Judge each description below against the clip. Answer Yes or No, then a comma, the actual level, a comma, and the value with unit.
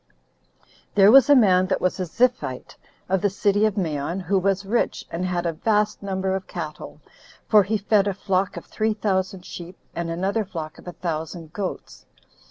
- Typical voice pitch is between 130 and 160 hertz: No, high, 190 Hz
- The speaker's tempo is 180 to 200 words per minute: Yes, average, 190 wpm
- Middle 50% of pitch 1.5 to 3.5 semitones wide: Yes, average, 2.8 semitones